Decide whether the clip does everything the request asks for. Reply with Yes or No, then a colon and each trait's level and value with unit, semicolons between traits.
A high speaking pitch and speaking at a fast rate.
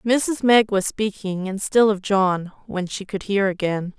No: high, 200 Hz; average, 195 wpm